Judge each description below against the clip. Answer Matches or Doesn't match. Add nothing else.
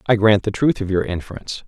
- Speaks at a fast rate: Matches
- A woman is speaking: Doesn't match